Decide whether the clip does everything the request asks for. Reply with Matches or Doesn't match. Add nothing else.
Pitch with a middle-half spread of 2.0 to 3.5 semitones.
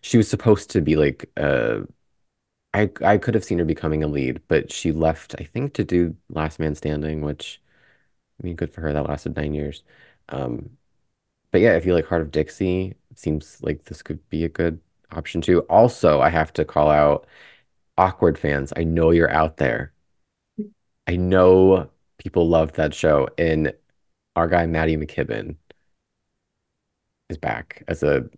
Matches